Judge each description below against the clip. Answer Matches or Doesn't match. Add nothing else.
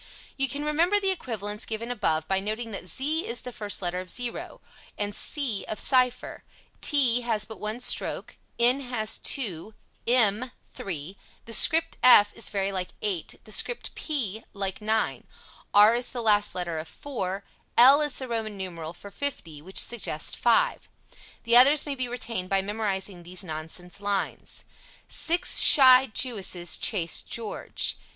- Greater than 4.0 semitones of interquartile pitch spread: Matches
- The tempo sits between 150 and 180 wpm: Matches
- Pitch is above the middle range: Matches